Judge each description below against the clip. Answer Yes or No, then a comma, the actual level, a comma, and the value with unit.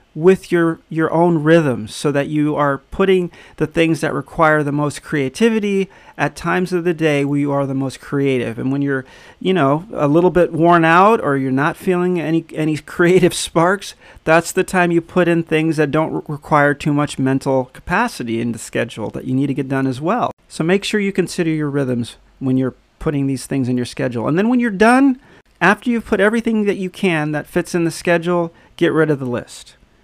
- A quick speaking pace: Yes, fast, 220 wpm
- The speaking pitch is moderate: Yes, medium, 160 Hz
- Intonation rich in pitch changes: No, average, 4.2 semitones